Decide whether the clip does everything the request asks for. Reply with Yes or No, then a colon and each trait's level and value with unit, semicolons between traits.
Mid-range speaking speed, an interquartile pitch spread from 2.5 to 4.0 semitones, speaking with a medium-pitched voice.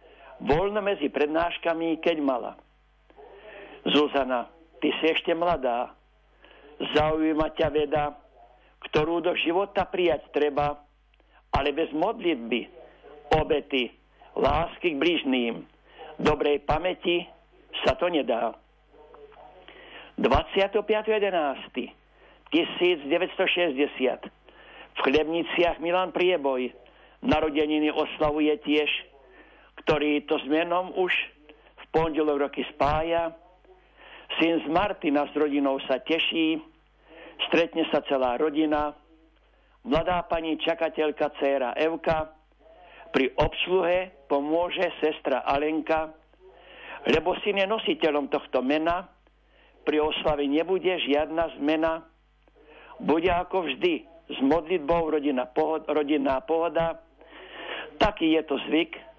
No: slow, 90 wpm; average, 2.8 semitones; medium, 160 Hz